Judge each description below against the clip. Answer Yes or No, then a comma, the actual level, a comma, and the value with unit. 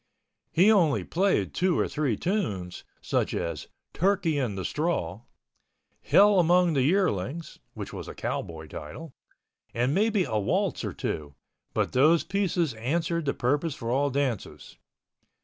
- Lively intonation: Yes, wide, 7.4 semitones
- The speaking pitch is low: No, medium, 150 Hz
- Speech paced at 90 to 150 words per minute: Yes, average, 145 wpm